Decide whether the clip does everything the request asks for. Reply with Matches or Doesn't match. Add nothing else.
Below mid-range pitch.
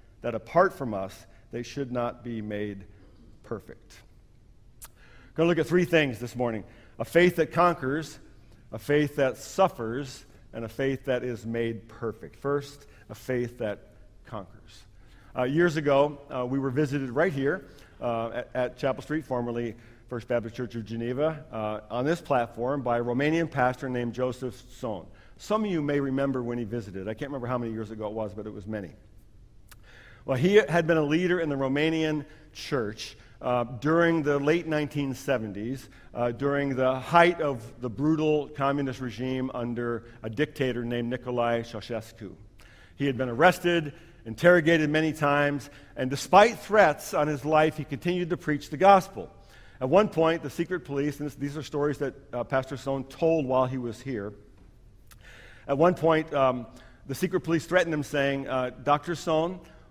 Matches